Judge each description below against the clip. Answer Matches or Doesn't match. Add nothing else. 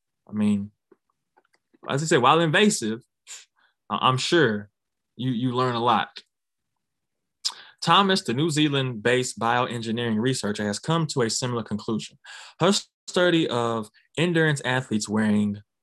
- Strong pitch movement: Matches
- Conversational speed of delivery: Doesn't match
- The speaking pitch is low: Matches